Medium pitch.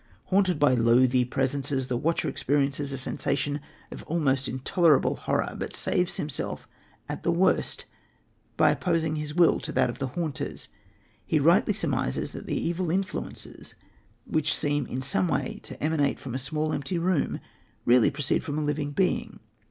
Yes: medium, 145 Hz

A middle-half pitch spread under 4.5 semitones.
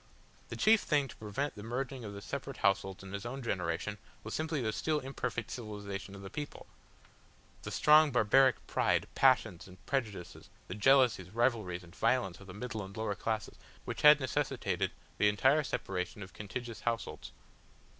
No: average, 5.1 semitones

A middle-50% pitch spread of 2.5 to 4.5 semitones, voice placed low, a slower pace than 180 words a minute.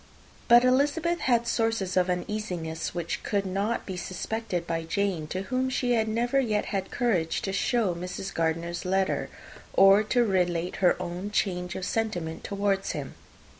No: average, 4.2 semitones; high, 195 Hz; average, 165 wpm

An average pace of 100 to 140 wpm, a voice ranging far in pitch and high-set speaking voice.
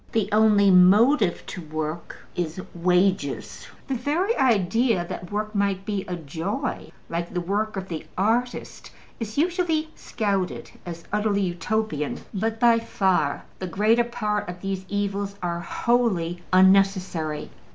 No: slow, 135 wpm; average, 3.8 semitones; high, 200 Hz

